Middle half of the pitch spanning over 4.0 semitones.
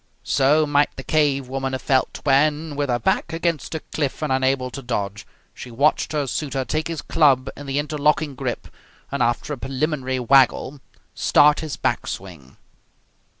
No: narrow, 2.5 semitones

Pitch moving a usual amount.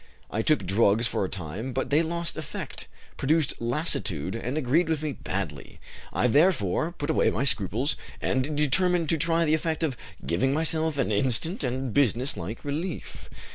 No: wide, 5.7 semitones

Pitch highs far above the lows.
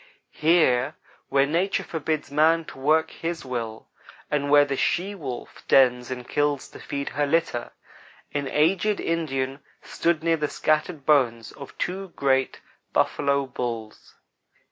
No: average, 3.5 semitones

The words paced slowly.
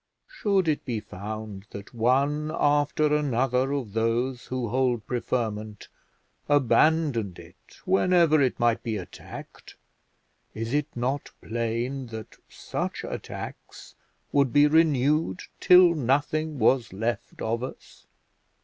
Yes: slow, 115 wpm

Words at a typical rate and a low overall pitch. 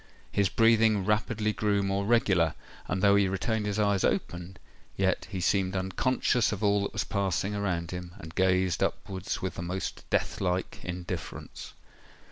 Yes: average, 160 wpm; very low, 95 Hz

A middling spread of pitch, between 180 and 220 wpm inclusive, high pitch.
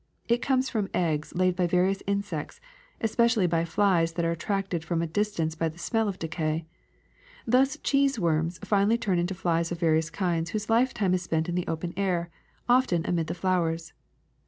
No: average, 3.7 semitones; average, 185 wpm; medium, 180 Hz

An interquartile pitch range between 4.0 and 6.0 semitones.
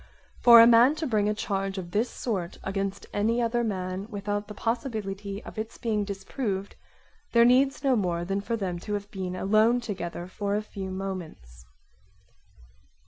No: average, 3.1 semitones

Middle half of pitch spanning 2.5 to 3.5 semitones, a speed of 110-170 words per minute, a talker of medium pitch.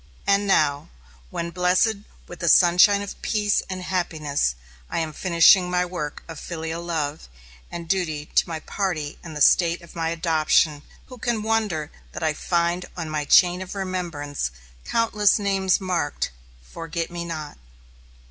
Yes: average, 2.9 semitones; average, 155 wpm; medium, 170 Hz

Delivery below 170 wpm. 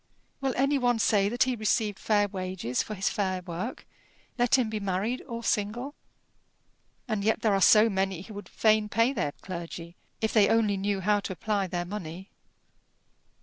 No: average, 180 wpm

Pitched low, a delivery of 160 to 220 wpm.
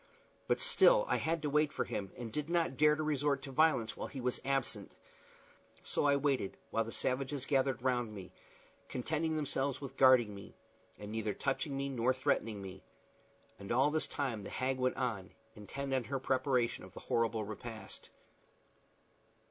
Yes: low, 130 Hz; average, 175 wpm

